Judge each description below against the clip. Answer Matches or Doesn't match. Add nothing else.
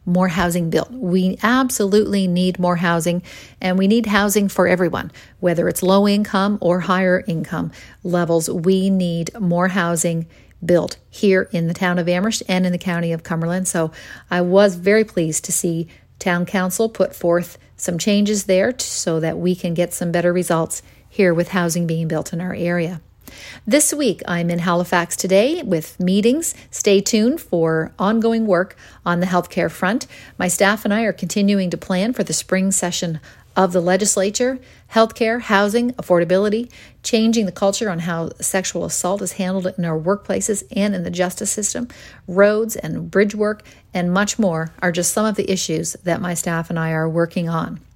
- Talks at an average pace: Matches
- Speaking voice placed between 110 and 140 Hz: Doesn't match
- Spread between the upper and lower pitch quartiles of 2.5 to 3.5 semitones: Matches